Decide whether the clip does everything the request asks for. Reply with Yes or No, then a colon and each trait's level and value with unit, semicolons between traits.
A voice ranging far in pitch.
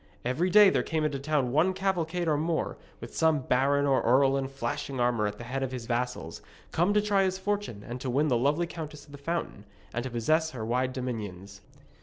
No: average, 4.8 semitones